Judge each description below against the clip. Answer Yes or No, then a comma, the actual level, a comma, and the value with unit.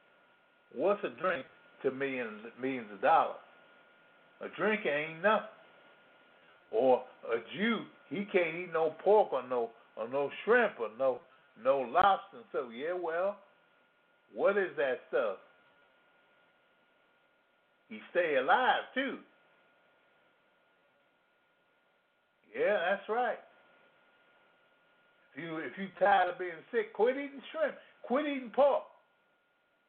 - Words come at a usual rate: No, slow, 115 wpm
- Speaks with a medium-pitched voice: No, high, 205 Hz